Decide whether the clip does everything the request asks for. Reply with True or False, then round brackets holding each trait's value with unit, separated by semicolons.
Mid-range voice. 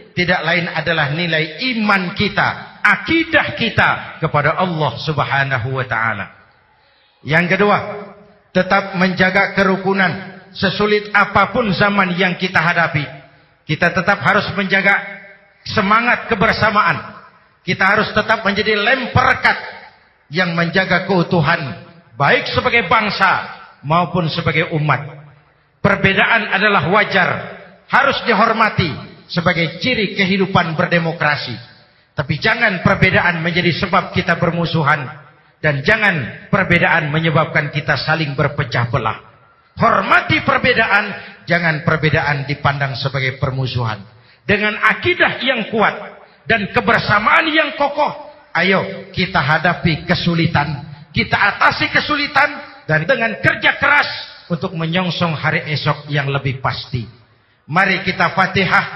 True (175 Hz)